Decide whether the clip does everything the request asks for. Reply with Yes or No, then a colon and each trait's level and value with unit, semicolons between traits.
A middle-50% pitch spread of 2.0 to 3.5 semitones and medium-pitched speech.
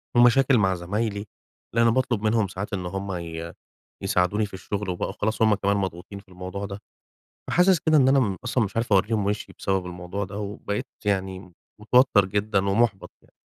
No: average, 2.8 semitones; low, 100 Hz